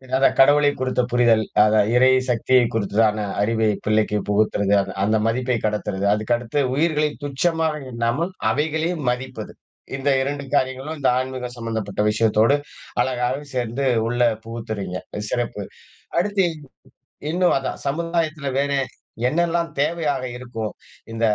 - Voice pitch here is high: No, low, 125 Hz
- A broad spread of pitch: No, average, 4.6 semitones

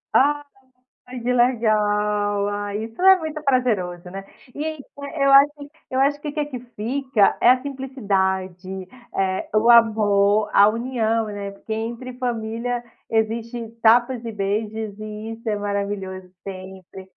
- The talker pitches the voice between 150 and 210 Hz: No, high, 220 Hz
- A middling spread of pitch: Yes, average, 3.7 semitones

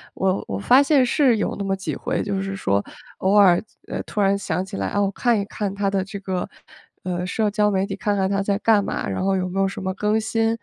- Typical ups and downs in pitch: No, narrow, 1.7 semitones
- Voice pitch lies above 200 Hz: No, high, 195 Hz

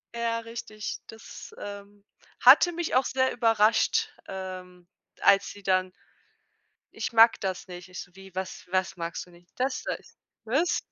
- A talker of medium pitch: No, high, 200 Hz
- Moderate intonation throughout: Yes, average, 3.9 semitones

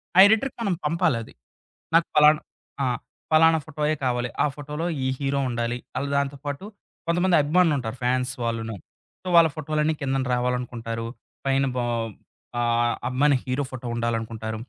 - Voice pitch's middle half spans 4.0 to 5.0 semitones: Yes, average, 4.3 semitones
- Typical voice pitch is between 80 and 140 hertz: Yes, low, 135 Hz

